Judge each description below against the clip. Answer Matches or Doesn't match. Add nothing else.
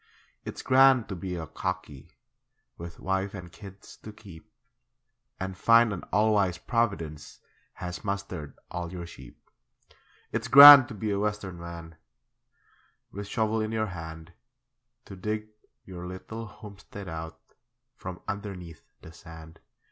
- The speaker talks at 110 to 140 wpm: Matches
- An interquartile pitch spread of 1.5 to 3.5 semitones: Doesn't match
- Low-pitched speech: Matches